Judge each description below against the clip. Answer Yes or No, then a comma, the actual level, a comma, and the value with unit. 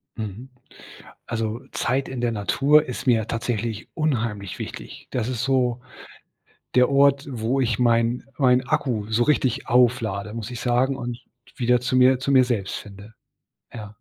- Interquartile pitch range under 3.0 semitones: Yes, narrow, 2.6 semitones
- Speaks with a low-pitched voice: Yes, low, 120 Hz